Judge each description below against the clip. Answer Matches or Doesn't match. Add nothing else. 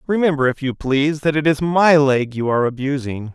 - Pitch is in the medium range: Matches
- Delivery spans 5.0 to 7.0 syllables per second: Matches